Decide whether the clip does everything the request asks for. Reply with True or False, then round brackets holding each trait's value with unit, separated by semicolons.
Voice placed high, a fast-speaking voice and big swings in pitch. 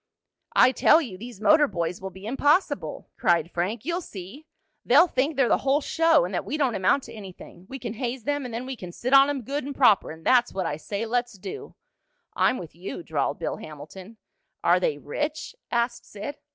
True (235 Hz; 210 wpm; 7.1 semitones)